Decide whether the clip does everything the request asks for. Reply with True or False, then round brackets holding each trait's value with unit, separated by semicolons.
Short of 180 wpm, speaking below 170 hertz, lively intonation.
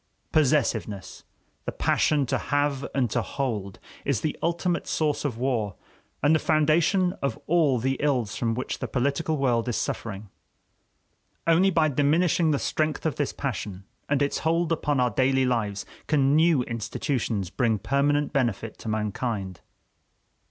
False (150 wpm; 140 Hz; 4.8 semitones)